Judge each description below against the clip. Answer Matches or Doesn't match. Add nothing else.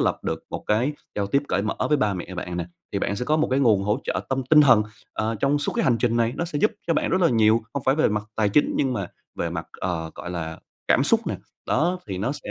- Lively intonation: Matches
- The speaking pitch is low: Matches